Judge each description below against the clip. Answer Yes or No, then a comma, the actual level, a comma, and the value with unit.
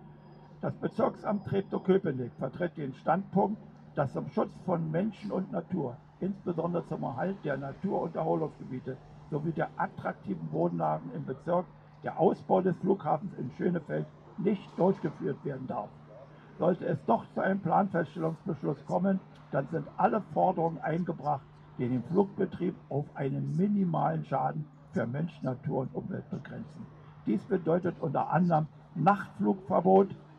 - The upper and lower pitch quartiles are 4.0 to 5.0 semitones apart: Yes, average, 4.4 semitones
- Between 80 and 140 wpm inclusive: Yes, average, 130 wpm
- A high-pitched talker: No, medium, 165 Hz